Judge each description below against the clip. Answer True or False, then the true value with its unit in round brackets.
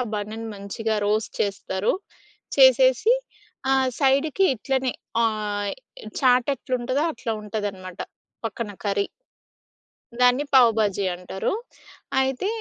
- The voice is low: False (225 Hz)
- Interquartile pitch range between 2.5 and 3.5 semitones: False (4.4 semitones)